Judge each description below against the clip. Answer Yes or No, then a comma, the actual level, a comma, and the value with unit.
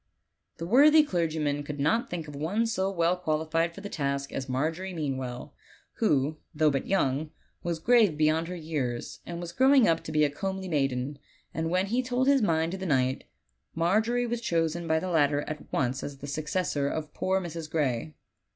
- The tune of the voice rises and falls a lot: No, average, 4.6 semitones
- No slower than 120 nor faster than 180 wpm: No, average, 190 wpm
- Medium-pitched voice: Yes, medium, 160 Hz